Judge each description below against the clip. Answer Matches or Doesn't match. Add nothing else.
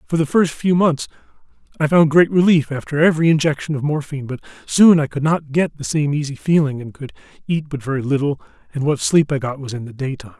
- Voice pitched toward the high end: Doesn't match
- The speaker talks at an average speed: Doesn't match